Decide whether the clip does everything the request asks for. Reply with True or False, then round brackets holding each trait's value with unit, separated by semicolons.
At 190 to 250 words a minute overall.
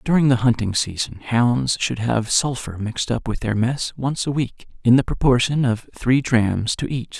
True (200 wpm)